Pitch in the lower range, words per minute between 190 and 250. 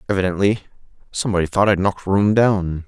No: very low, 95 Hz; average, 145 wpm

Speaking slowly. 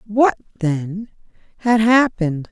Yes: slow, 95 wpm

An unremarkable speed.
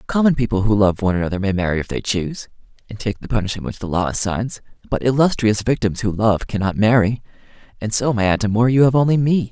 No: fast, 220 wpm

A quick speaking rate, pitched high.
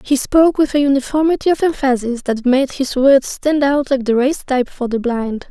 Yes: fast, 220 wpm; very high, 270 Hz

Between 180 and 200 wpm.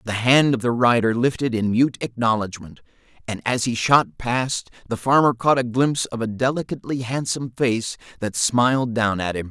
Yes: average, 185 wpm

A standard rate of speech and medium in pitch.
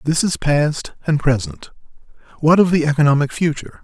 Yes: average, 155 wpm; medium, 155 Hz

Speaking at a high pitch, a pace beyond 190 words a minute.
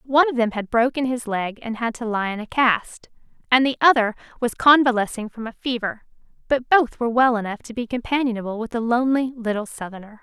Yes: high, 235 Hz; average, 200 wpm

